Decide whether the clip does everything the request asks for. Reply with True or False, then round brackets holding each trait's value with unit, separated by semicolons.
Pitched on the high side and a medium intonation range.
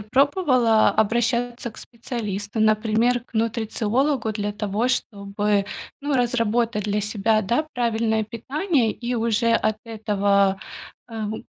False (225 Hz; 2.3 semitones)